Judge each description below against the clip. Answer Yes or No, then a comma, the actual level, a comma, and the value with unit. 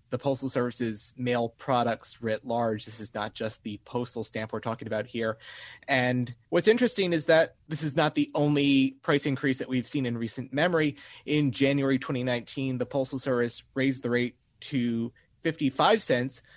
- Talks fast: No, average, 175 wpm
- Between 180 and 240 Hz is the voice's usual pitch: No, low, 125 Hz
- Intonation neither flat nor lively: Yes, average, 3.3 semitones